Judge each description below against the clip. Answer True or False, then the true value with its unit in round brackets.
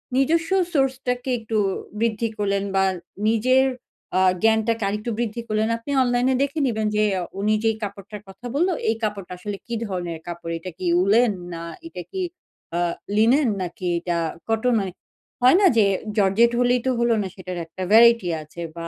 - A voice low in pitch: False (220 Hz)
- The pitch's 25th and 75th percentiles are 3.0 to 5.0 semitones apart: True (3.9 semitones)